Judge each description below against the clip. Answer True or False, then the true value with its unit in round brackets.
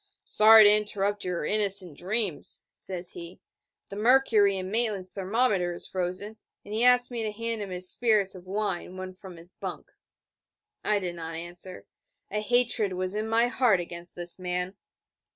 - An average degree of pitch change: True (3.1 semitones)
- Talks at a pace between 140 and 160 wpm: False (170 wpm)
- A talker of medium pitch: False (195 Hz)